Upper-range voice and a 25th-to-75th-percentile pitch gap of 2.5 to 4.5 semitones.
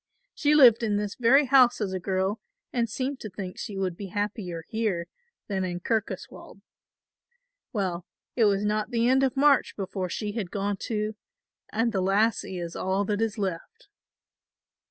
Yes: high, 210 Hz; average, 3.5 semitones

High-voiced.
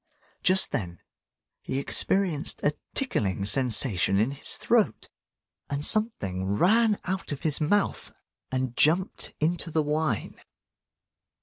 No: medium, 145 Hz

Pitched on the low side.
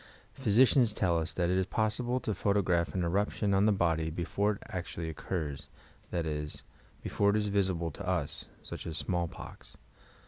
Yes: very low, 90 Hz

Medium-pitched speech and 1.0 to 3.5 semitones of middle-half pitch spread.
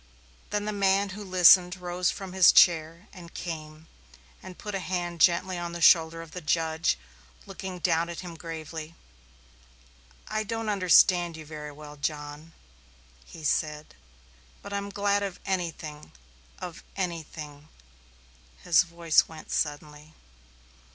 Yes: medium, 170 Hz; average, 2.9 semitones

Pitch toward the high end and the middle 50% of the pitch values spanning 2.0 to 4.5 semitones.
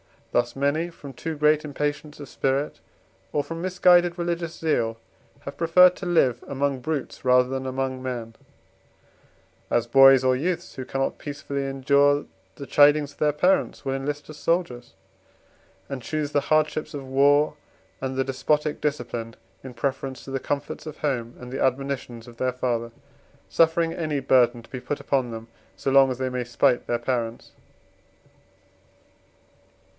No: low, 135 Hz; average, 2.8 semitones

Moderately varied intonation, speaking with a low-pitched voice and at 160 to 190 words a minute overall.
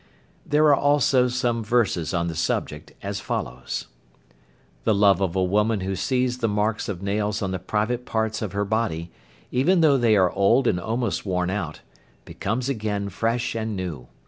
Yes: average, 4.4 semitones; low, 105 Hz; average, 175 wpm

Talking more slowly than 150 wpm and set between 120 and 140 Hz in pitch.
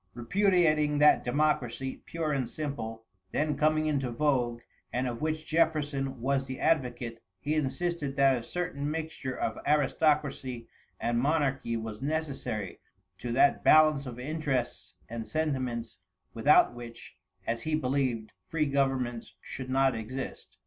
Yes: slow, 135 wpm; low, 135 Hz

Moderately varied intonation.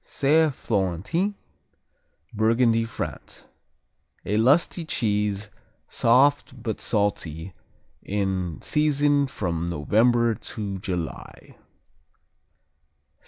No: wide, 5.9 semitones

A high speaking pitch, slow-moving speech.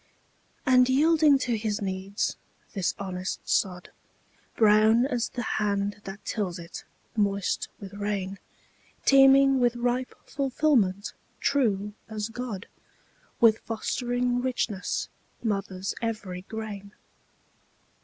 Yes: high, 215 Hz; slow, 105 wpm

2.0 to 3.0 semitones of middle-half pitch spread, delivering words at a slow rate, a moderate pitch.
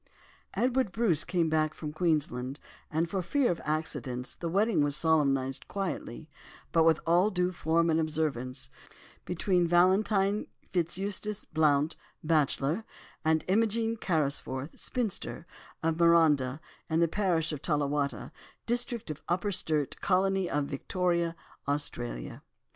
No: average, 4.0 semitones; slow, 125 wpm; medium, 165 Hz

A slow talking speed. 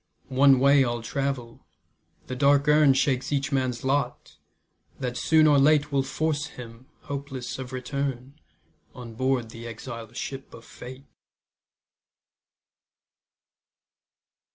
Yes: slow, 115 wpm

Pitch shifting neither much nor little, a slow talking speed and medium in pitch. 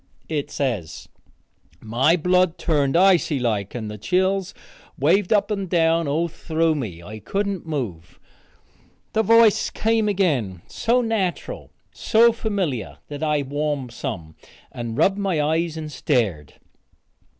No: wide, 7.6 semitones; slow, 130 wpm; medium, 160 Hz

